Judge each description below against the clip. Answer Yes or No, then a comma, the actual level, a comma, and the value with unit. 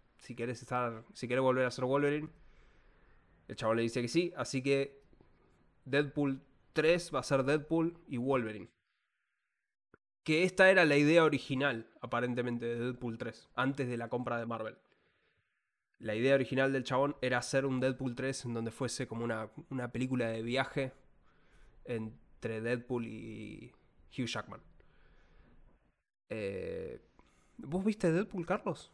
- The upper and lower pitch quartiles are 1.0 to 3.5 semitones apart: Yes, average, 3.2 semitones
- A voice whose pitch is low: Yes, low, 130 Hz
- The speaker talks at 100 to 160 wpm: Yes, average, 145 wpm